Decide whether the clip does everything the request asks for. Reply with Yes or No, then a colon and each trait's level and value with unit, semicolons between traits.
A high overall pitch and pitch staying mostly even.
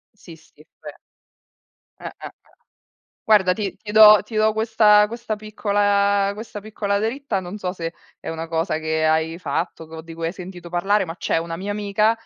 No: high, 200 Hz; average, 4.2 semitones